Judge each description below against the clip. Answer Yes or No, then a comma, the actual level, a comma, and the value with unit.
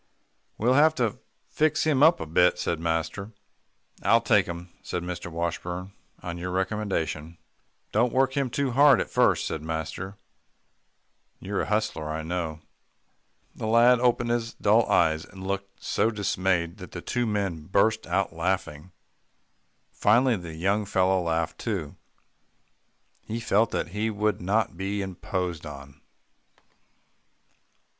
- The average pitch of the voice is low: Yes, very low, 95 Hz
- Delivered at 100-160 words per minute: Yes, average, 140 wpm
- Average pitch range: Yes, average, 4.6 semitones